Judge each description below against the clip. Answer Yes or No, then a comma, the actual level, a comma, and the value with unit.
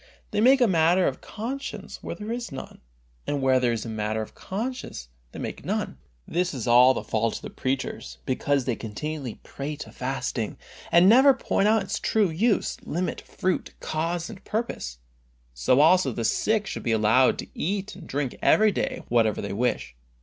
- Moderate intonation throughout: No, wide, 9.0 semitones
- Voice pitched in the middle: Yes, medium, 150 Hz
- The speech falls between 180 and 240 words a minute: Yes, average, 185 wpm